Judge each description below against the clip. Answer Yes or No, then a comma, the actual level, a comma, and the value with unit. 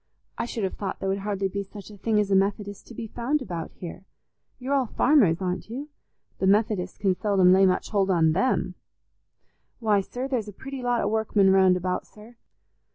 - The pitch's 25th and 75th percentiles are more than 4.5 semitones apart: No, average, 3.2 semitones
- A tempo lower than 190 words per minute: No, fast, 205 wpm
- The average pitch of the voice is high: Yes, high, 200 Hz